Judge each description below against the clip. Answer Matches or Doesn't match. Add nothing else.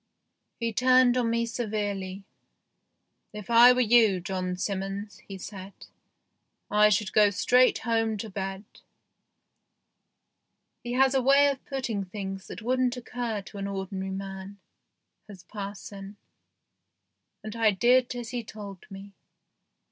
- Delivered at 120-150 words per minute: Matches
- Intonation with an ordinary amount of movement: Matches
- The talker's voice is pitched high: Matches